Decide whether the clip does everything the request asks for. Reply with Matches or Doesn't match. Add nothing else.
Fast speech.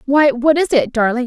Matches